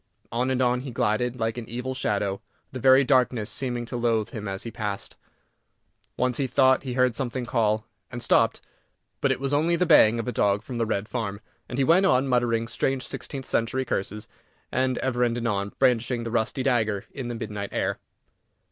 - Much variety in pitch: No, average, 2.7 semitones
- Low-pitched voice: Yes, low, 120 Hz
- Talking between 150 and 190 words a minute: No, average, 200 wpm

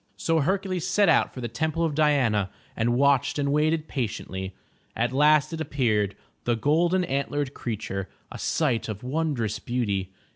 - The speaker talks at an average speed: Yes, average, 160 wpm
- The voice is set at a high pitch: No, medium, 140 Hz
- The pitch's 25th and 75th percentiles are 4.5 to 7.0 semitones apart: Yes, wide, 5.5 semitones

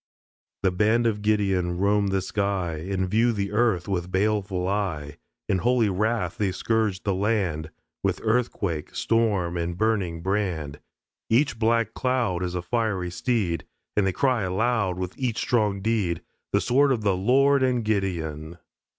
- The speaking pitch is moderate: No, low, 100 Hz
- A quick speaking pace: No, average, 155 wpm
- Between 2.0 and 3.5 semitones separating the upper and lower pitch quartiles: No, average, 3.9 semitones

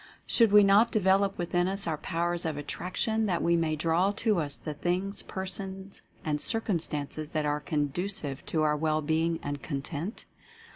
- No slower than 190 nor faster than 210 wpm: No, average, 165 wpm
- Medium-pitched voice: Yes, medium, 170 Hz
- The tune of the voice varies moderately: Yes, average, 4.2 semitones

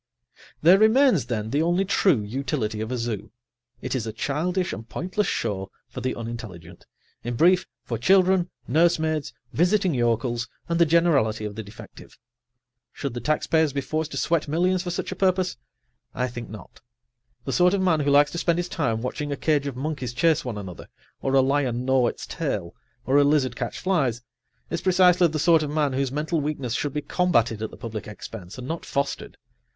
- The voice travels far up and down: Yes, wide, 6.2 semitones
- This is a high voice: No, medium, 140 Hz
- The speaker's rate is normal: Yes, average, 195 wpm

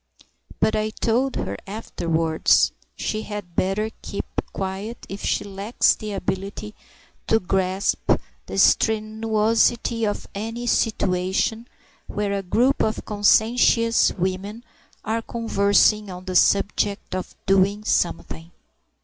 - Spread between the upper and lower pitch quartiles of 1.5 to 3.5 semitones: Yes, narrow, 2.5 semitones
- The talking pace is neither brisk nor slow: No, slow, 115 wpm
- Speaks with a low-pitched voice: No, high, 210 Hz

